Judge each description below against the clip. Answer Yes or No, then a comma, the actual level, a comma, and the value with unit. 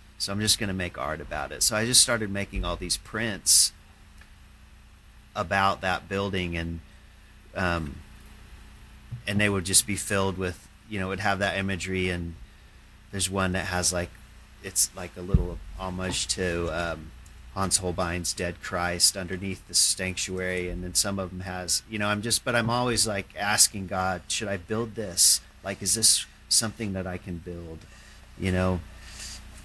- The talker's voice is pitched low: Yes, very low, 95 Hz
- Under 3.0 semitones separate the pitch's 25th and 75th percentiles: Yes, narrow, 2.5 semitones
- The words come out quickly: No, average, 175 wpm